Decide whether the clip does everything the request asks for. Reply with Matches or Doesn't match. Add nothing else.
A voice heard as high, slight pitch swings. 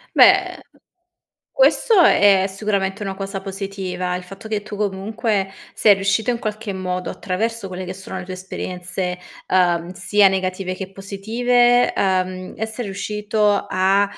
Matches